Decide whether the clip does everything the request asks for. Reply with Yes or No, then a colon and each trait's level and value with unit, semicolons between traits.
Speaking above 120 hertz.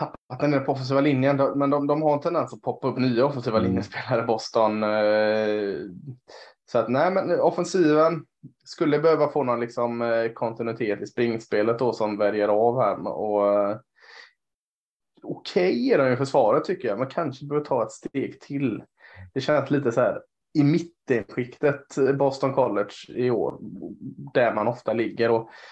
Yes: low, 130 Hz